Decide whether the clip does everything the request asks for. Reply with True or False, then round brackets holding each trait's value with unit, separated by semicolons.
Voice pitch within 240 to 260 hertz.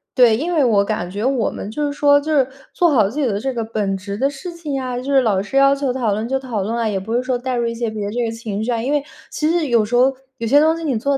True (245 Hz)